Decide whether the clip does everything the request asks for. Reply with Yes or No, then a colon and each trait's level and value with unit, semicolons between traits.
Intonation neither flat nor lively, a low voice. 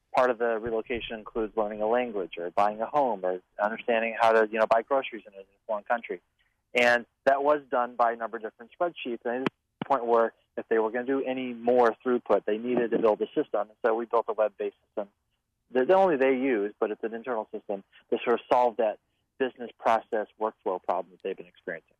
No: narrow, 2.3 semitones; low, 115 Hz